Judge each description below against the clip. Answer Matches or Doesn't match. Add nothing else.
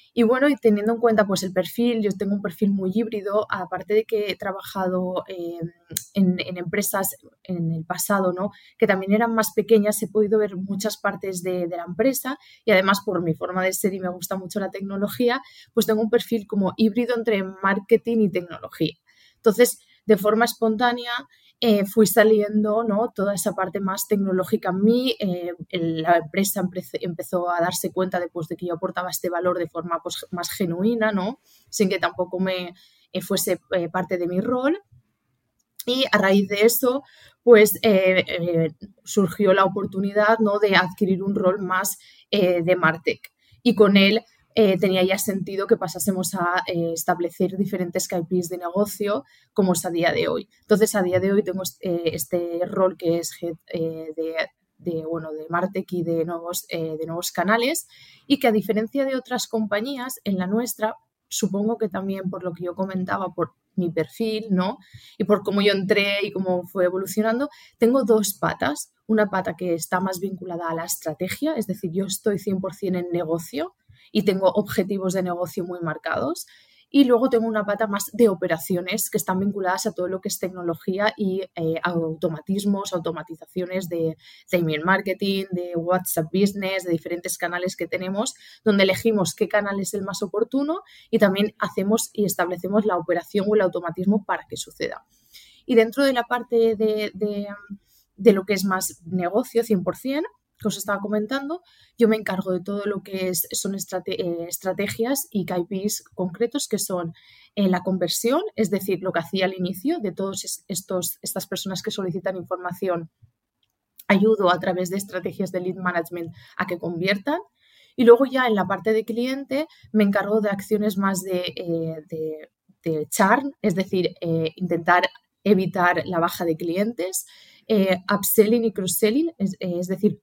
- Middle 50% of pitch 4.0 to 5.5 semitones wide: Doesn't match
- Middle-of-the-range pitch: Doesn't match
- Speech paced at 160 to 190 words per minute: Matches